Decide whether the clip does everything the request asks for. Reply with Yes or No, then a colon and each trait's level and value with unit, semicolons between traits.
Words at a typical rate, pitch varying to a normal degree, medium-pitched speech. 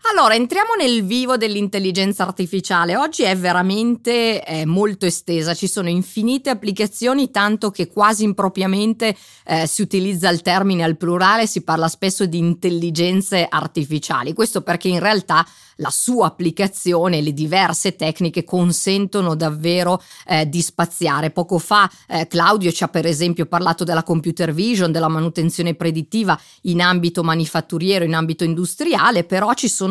Yes: average, 145 wpm; average, 3.4 semitones; medium, 180 Hz